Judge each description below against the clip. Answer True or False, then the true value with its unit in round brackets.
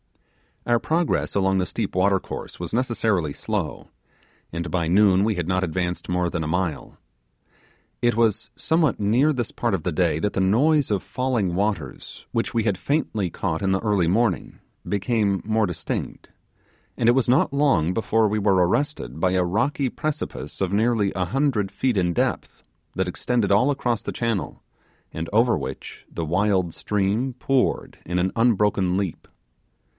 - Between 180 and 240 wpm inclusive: False (170 wpm)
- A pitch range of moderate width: True (4.6 semitones)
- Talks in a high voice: False (100 Hz)